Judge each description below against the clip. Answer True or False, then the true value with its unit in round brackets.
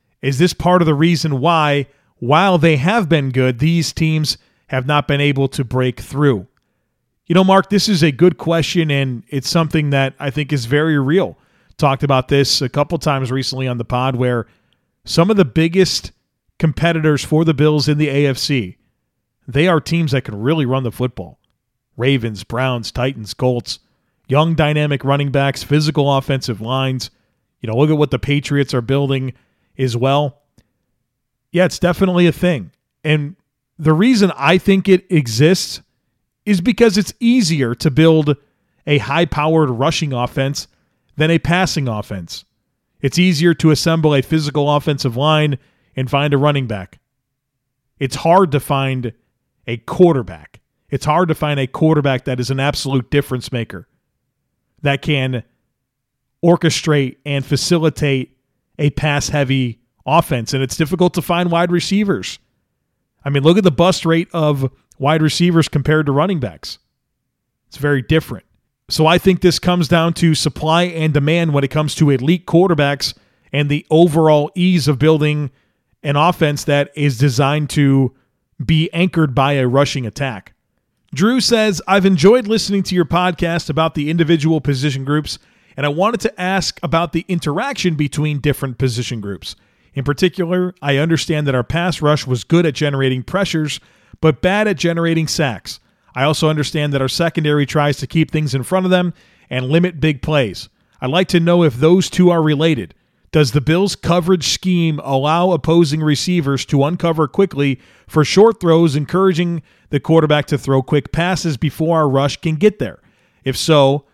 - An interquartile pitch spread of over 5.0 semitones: False (3.8 semitones)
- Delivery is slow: False (165 wpm)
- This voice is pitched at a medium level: True (150 Hz)